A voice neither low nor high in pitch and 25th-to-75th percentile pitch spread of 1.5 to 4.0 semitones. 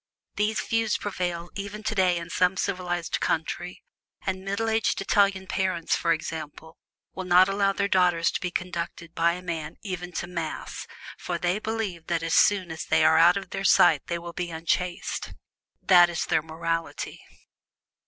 Yes: medium, 180 Hz; narrow, 2.5 semitones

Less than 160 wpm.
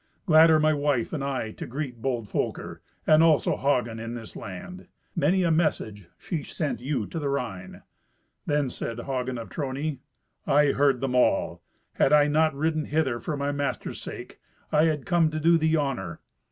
No: average, 180 wpm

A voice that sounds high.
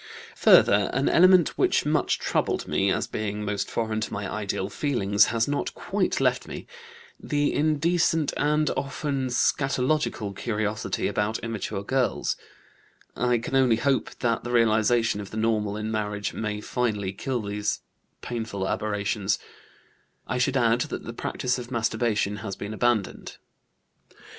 No: low, 115 Hz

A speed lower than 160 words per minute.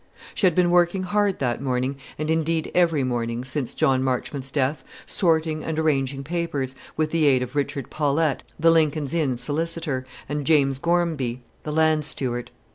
No: average, 165 wpm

